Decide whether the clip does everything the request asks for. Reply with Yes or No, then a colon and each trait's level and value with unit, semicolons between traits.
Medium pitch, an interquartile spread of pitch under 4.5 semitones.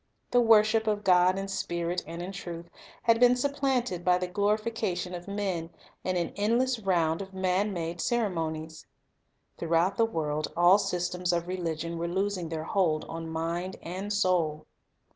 Yes: medium, 180 Hz; average, 3.3 semitones